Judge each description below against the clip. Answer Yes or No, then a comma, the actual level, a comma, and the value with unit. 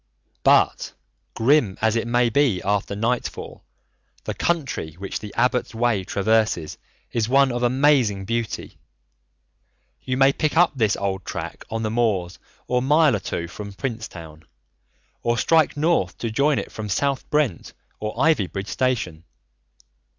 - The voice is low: Yes, low, 115 Hz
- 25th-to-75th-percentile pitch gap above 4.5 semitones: Yes, average, 5.1 semitones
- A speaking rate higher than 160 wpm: No, average, 145 wpm